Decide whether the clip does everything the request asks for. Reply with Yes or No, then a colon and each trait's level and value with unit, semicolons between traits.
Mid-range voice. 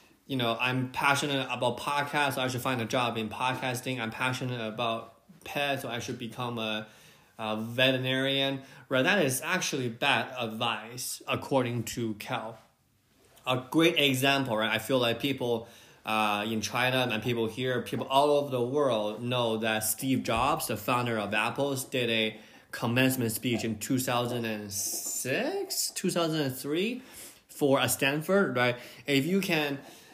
No: low, 125 Hz